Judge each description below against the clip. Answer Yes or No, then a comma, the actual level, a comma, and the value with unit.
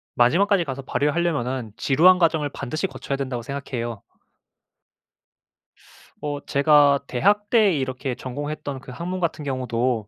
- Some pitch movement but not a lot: Yes, average, 4.5 semitones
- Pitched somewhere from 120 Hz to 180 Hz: Yes, medium, 140 Hz